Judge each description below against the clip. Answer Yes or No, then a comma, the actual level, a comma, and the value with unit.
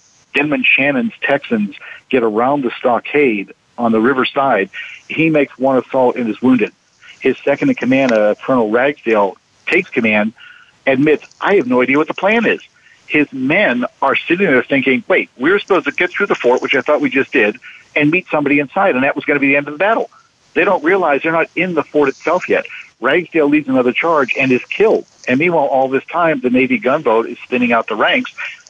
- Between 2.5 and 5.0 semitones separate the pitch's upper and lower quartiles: Yes, average, 4.3 semitones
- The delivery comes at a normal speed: No, fast, 210 wpm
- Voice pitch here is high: No, medium, 140 Hz